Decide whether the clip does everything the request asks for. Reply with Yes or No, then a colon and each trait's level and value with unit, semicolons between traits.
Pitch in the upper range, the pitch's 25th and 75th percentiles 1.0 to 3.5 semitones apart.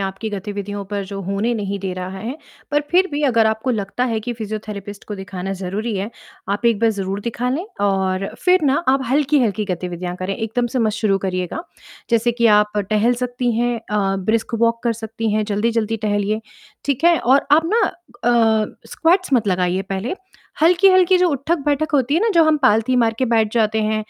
No: high, 220 Hz; average, 4.2 semitones